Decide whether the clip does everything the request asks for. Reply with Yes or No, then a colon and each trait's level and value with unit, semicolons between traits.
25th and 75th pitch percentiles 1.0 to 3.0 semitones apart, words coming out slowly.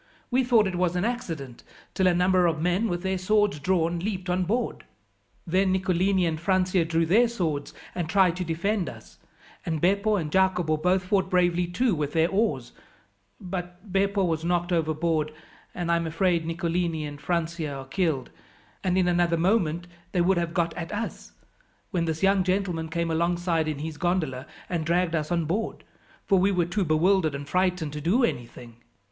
No: narrow, 2.6 semitones; average, 185 wpm